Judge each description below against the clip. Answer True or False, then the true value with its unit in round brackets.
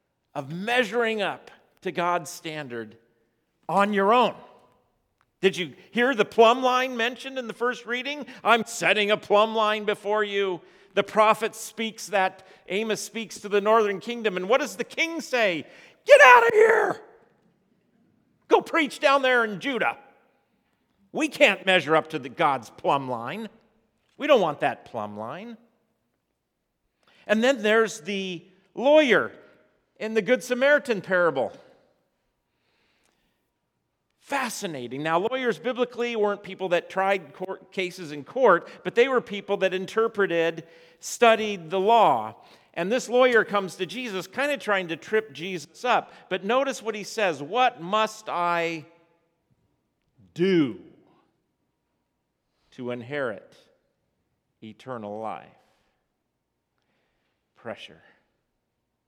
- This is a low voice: False (205 Hz)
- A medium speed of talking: False (130 wpm)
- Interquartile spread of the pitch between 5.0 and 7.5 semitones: True (5.5 semitones)